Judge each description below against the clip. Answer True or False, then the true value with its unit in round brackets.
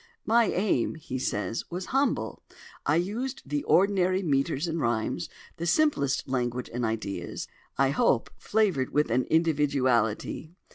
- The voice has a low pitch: False (150 Hz)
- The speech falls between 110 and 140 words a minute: True (135 wpm)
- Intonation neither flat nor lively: False (6.8 semitones)